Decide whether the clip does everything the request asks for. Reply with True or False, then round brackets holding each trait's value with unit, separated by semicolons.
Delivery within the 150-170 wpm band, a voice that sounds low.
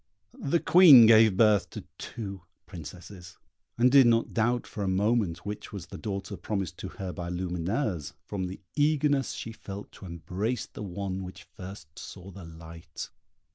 True (165 wpm; 100 Hz)